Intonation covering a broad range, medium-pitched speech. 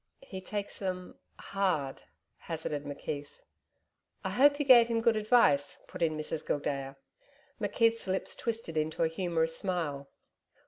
Yes: wide, 6.2 semitones; medium, 175 Hz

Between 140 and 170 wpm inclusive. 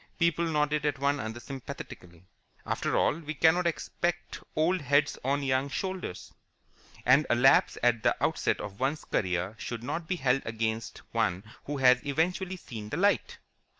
Yes: average, 160 wpm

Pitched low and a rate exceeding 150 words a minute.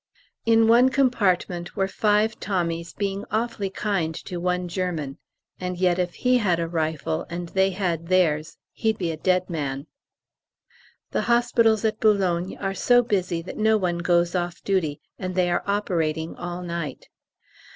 No: medium, 180 Hz; average, 160 wpm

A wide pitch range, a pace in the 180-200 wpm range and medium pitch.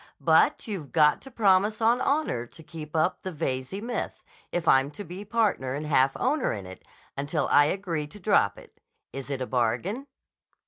Yes: wide, 7.1 semitones; average, 185 wpm; medium, 160 Hz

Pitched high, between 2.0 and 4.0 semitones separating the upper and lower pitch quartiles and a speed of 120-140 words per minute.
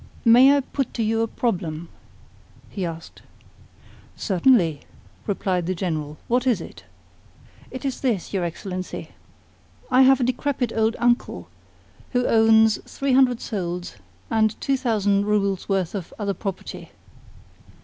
No: high, 215 Hz; average, 5.2 semitones; slow, 135 wpm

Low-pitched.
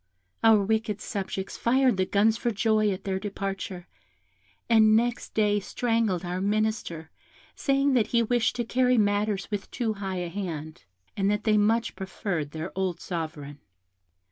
No: high, 205 Hz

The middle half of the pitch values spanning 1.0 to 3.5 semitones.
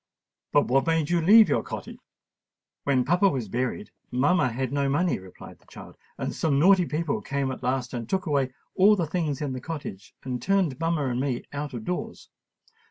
No: average, 4.7 semitones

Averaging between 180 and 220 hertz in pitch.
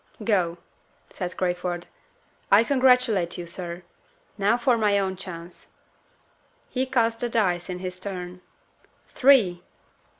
Yes: high, 190 Hz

